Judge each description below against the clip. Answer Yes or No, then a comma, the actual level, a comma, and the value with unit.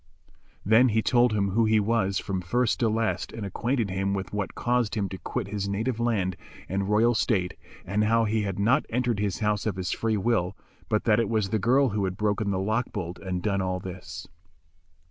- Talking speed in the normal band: No, fast, 215 wpm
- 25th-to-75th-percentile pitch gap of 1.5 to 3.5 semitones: Yes, average, 2.8 semitones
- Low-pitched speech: Yes, low, 105 Hz